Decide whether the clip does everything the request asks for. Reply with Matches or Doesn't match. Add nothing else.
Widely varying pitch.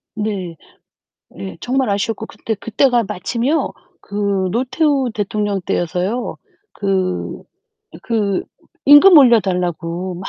Doesn't match